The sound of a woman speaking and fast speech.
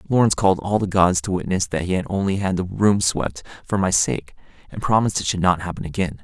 No: male; fast, 240 wpm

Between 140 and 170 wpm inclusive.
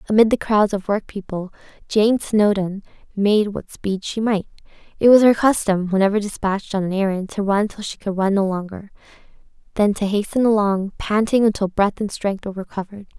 No: average, 180 wpm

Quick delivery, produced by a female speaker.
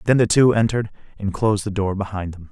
No: fast, 240 wpm; male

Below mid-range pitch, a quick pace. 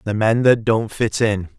Yes: low, 110 Hz; fast, 230 wpm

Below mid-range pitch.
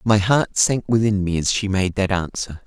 Yes: low, 100 Hz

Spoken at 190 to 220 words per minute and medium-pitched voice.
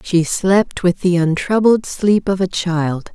No: average, 170 wpm; medium, 180 Hz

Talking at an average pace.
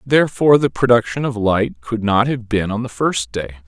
No: fast, 210 wpm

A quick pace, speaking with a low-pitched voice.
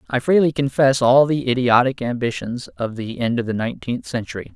No: average, 185 wpm; low, 125 Hz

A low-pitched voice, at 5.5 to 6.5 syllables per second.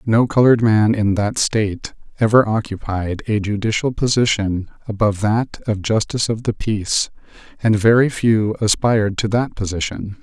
No: low, 110 Hz; 5.0 syllables/s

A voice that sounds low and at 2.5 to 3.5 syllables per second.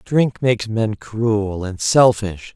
Yes: low, 110 Hz; 3.3 syllables/s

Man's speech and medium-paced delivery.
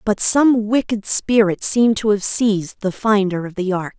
No: female; average, 195 wpm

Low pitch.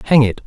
Yes: low, 130 Hz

